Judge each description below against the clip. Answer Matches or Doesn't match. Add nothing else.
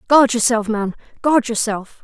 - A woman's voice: Matches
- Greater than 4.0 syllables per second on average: Matches